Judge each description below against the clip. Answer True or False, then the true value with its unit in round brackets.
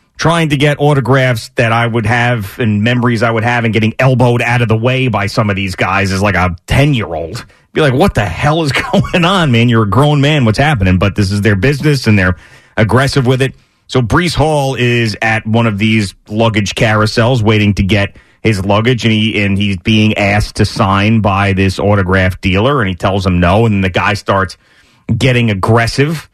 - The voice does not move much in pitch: False (4.0 semitones)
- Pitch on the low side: True (115 Hz)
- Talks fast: True (215 wpm)